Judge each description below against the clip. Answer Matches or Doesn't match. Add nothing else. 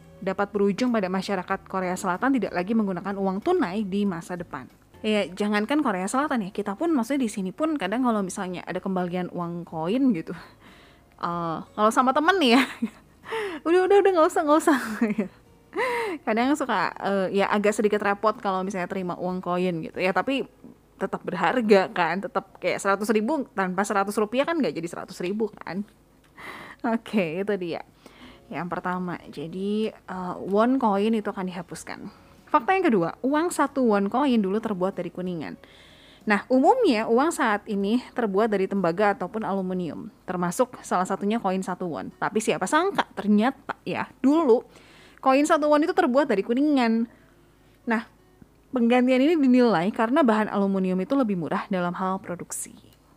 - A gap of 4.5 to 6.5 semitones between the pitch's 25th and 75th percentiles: Matches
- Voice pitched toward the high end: Matches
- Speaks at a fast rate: Matches